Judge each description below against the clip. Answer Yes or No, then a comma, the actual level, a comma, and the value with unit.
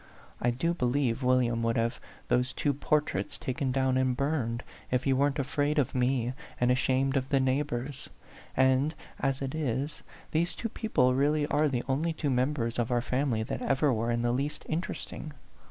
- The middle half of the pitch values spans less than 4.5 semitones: Yes, average, 2.7 semitones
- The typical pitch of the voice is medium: No, low, 130 Hz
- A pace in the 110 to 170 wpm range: No, average, 185 wpm